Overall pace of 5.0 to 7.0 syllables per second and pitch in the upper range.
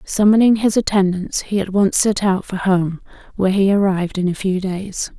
Yes: 5.1 syllables/s; high, 195 Hz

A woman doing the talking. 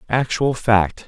No: male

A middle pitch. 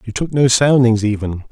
No: low, 120 Hz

